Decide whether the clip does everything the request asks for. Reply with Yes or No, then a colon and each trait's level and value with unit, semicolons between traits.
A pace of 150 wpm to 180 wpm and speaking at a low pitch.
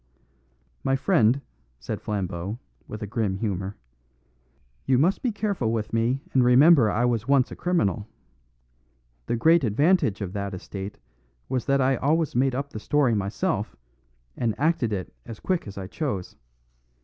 Yes: average, 155 wpm; low, 120 Hz